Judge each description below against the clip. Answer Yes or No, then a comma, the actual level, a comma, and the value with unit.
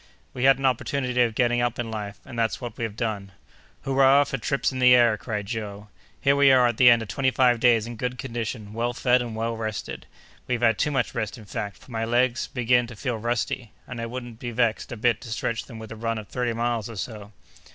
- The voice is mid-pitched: No, low, 120 Hz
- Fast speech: Yes, fast, 245 wpm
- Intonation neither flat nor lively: No, narrow, 2.0 semitones